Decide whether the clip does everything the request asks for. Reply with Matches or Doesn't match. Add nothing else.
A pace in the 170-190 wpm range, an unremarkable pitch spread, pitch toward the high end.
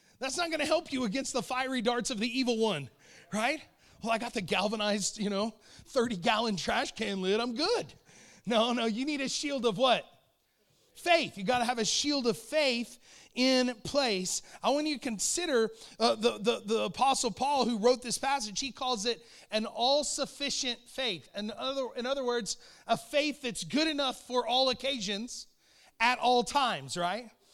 Matches